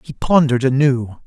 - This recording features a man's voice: Yes, male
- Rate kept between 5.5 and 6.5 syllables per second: No, 5.2 syllables/s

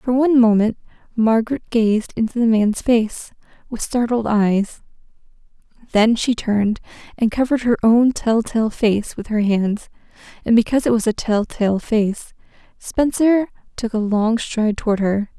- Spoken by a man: No, female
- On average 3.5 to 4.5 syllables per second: No, 4.8 syllables/s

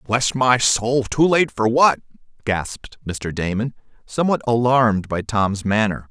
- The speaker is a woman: No, male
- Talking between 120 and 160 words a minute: Yes, average, 145 wpm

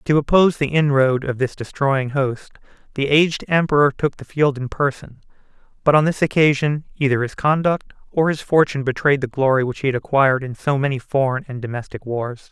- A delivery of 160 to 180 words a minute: No, average, 190 wpm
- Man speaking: Yes, male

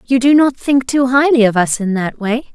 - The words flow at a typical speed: No, fast, 260 wpm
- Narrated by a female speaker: Yes, female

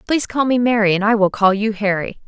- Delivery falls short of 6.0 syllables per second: No, 6.3 syllables/s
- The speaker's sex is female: Yes, female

